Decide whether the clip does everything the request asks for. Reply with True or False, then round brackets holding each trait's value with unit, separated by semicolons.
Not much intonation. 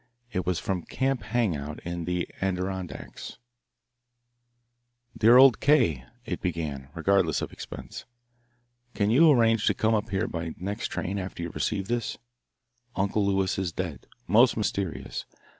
False (4.3 semitones)